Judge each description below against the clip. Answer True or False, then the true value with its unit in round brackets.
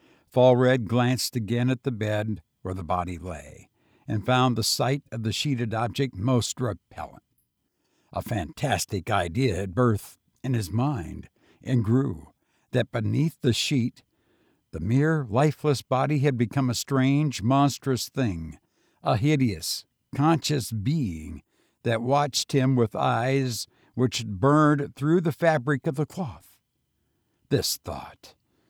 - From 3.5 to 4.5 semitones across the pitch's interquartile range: True (3.9 semitones)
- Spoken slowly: True (130 wpm)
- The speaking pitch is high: False (125 Hz)